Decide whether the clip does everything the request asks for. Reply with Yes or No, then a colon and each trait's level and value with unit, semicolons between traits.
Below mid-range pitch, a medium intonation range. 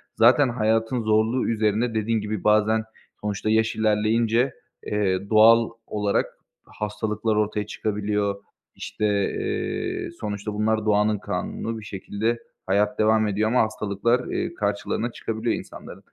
No: low, 110 Hz; narrow, 1.3 semitones